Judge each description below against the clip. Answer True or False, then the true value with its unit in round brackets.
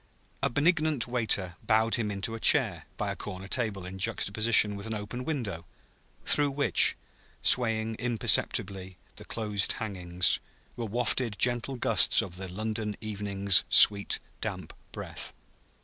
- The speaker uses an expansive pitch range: False (3.5 semitones)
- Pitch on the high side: False (110 Hz)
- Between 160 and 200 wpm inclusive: False (135 wpm)